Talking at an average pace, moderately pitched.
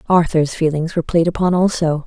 Yes: average, 175 wpm; medium, 165 Hz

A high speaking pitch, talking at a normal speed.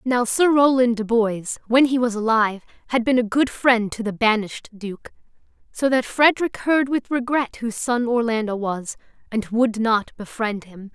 Yes: high, 235 Hz; average, 180 wpm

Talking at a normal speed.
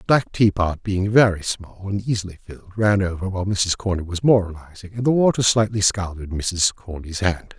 Yes: average, 190 wpm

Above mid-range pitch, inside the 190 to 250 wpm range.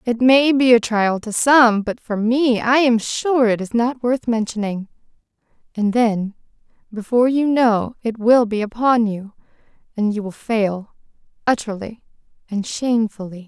No: high, 230 Hz; average, 155 wpm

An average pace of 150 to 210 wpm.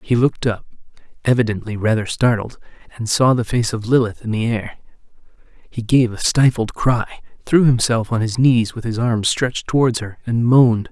Yes: average, 180 wpm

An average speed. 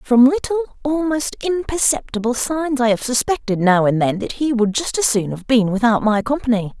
Yes: average, 195 wpm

